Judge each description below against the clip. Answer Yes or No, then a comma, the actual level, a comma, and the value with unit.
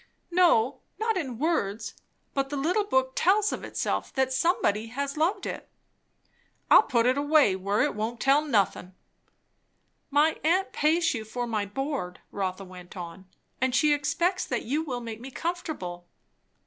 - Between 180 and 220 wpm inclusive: No, average, 160 wpm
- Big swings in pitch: Yes, wide, 6.5 semitones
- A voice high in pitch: Yes, very high, 265 Hz